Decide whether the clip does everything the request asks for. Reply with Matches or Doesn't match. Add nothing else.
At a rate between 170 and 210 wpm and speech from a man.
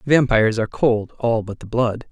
Matches